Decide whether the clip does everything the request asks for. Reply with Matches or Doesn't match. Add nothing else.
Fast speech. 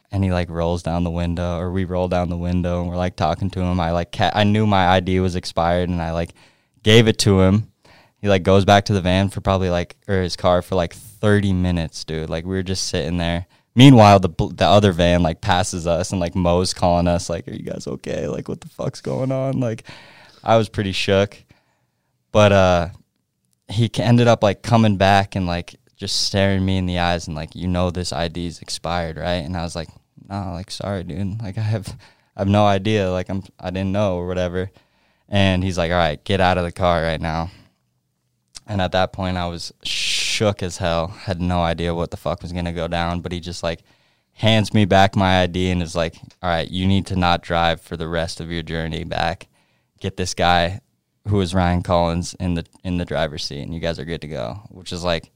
Matches